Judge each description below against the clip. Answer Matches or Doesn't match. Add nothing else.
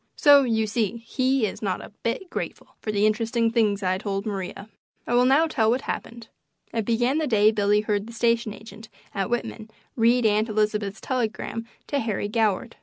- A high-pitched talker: Matches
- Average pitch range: Doesn't match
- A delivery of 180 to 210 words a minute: Matches